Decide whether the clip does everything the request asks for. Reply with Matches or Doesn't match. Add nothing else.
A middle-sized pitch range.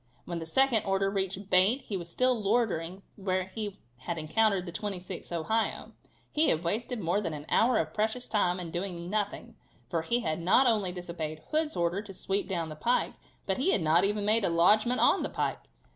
Matches